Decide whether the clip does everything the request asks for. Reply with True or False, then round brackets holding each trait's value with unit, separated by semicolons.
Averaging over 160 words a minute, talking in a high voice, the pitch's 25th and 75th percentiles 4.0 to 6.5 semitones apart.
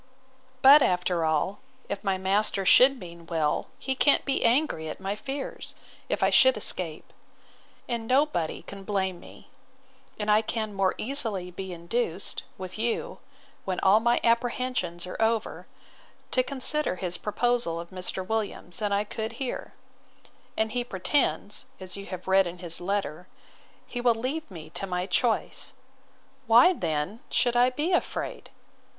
False (155 wpm; 205 Hz; 5.0 semitones)